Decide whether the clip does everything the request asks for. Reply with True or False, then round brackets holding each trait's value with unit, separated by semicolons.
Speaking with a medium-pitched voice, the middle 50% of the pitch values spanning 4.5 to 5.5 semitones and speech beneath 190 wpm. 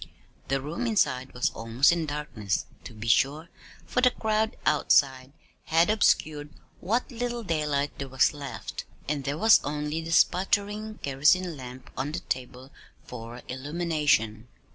True (150 Hz; 5.2 semitones; 140 wpm)